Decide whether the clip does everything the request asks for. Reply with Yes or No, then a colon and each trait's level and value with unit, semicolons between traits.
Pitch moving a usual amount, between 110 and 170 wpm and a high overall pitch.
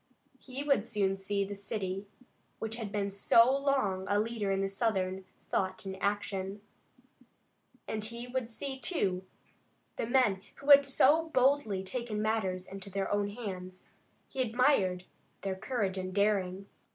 Yes: average, 3.9 semitones; average, 145 wpm; high, 205 Hz